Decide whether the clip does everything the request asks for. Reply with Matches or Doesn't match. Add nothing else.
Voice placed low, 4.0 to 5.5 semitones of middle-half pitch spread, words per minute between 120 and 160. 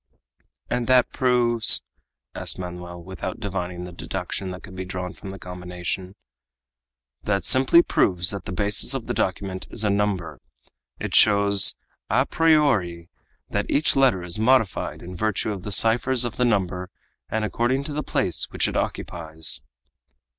Matches